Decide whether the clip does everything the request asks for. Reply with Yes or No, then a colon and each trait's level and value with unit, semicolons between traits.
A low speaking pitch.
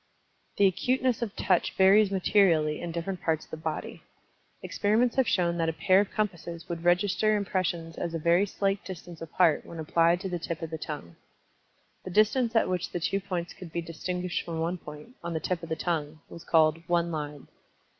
No: medium, 175 Hz